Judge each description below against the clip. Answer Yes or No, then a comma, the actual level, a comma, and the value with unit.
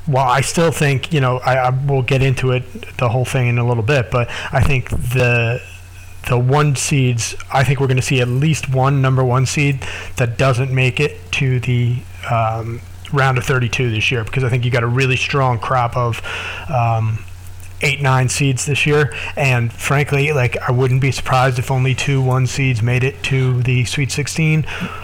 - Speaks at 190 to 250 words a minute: Yes, average, 200 wpm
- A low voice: Yes, low, 130 Hz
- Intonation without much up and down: Yes, narrow, 2.1 semitones